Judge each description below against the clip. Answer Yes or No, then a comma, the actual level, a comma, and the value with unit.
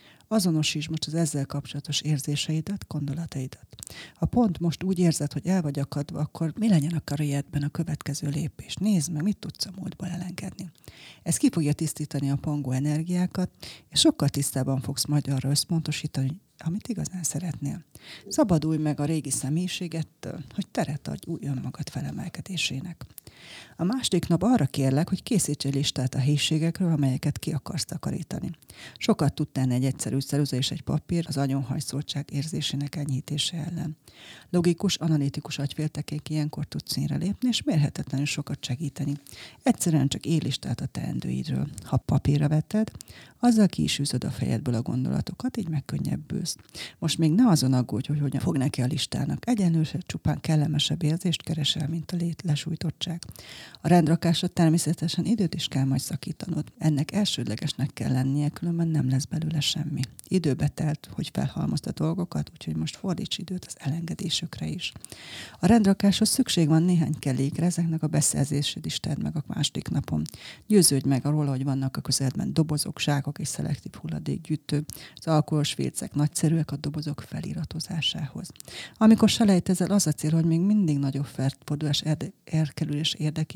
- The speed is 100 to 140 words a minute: No, average, 150 wpm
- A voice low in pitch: No, medium, 155 Hz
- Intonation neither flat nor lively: Yes, average, 3.3 semitones